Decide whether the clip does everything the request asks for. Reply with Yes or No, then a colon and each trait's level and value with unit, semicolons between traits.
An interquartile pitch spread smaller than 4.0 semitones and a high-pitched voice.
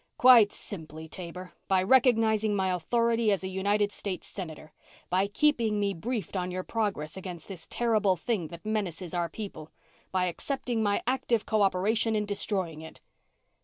Yes: average, 3.4 semitones; high, 200 Hz